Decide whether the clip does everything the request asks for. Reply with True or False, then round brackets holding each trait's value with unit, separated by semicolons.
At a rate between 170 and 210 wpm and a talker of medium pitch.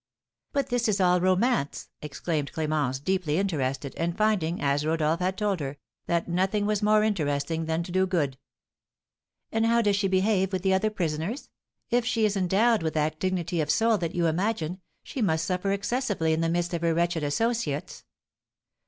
True (185 wpm; 180 Hz)